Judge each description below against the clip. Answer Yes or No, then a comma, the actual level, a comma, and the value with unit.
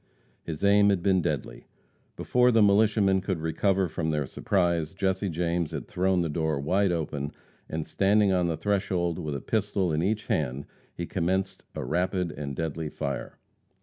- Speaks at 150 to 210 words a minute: Yes, average, 170 wpm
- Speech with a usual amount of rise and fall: Yes, average, 3.7 semitones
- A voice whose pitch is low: Yes, very low, 90 Hz